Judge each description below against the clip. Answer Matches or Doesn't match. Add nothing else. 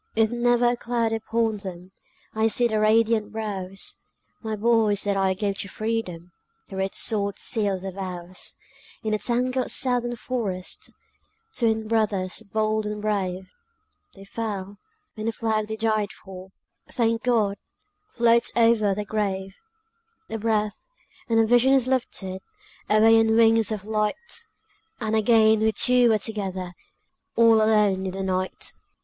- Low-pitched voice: Doesn't match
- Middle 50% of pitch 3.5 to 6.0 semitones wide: Doesn't match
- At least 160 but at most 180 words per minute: Doesn't match